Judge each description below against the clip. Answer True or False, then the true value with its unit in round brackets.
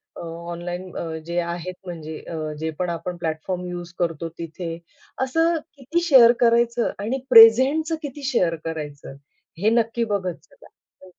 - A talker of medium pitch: True (180 Hz)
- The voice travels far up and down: True (6.0 semitones)